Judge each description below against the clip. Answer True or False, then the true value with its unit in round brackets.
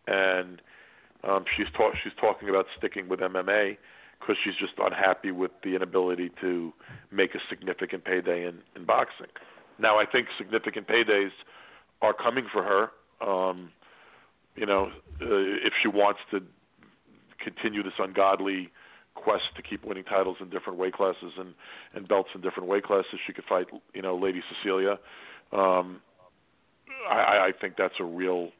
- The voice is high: False (95 Hz)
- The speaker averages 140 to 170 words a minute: True (155 wpm)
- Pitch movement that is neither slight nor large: False (1.2 semitones)